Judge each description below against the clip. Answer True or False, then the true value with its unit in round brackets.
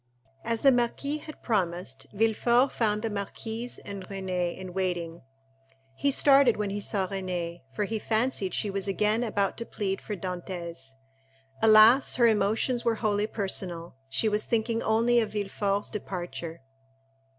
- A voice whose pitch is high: True (205 Hz)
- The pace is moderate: True (150 wpm)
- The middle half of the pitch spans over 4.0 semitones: False (3.5 semitones)